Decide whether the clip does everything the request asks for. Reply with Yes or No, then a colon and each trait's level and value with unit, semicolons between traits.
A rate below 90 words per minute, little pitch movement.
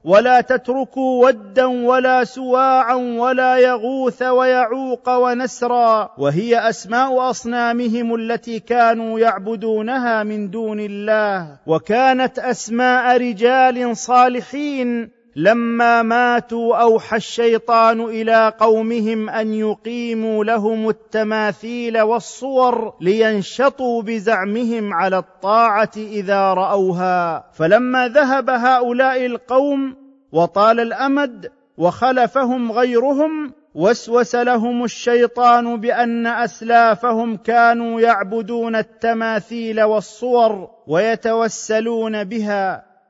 Yes: average, 80 wpm; narrow, 2.2 semitones